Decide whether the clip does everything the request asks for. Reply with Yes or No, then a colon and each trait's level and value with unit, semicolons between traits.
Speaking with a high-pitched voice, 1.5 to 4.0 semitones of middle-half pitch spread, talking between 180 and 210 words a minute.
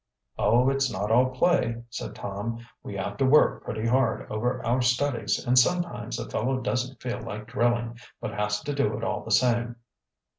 No: low, 120 Hz; average, 2.8 semitones; average, 185 wpm